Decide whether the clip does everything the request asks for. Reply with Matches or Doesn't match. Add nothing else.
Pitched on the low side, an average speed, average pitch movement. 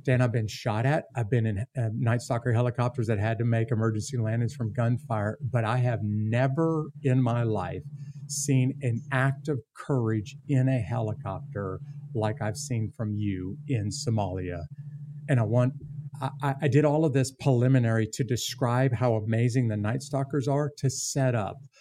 Matches